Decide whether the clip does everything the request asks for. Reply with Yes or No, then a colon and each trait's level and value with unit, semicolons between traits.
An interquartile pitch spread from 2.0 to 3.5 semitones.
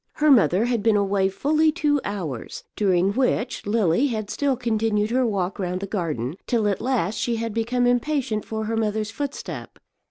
No: average, 3.9 semitones